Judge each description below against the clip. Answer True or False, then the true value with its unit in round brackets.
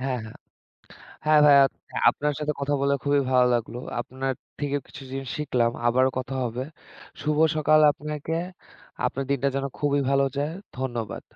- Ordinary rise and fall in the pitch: False (2.2 semitones)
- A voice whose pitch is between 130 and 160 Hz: True (140 Hz)